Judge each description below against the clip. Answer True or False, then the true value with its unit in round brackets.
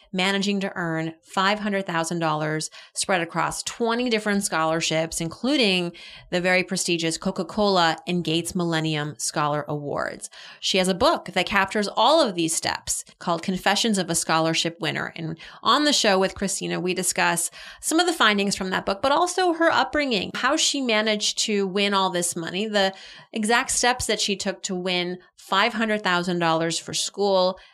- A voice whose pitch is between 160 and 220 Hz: True (190 Hz)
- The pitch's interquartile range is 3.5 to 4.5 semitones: True (3.9 semitones)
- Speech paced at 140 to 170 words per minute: True (160 wpm)